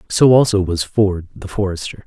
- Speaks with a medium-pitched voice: No, very low, 95 Hz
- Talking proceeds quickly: No, average, 175 wpm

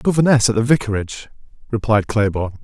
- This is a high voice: No, low, 115 Hz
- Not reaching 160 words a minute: Yes, slow, 135 wpm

